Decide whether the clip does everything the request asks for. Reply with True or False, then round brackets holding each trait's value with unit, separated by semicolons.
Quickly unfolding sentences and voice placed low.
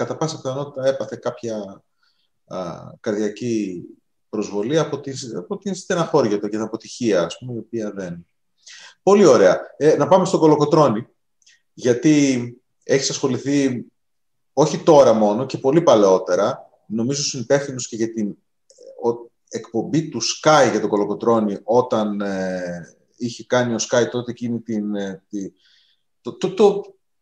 False (140 wpm; 120 Hz)